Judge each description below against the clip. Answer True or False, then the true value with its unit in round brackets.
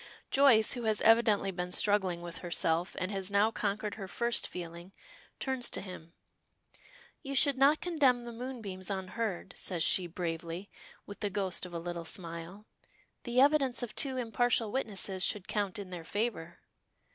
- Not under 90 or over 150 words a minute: False (160 wpm)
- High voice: True (200 Hz)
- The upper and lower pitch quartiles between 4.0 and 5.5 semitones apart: True (4.9 semitones)